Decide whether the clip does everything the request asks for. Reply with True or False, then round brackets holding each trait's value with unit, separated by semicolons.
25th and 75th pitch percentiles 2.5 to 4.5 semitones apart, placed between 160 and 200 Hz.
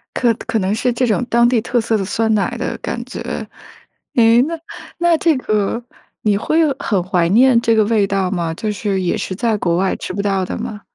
False (3.5 semitones; 220 Hz)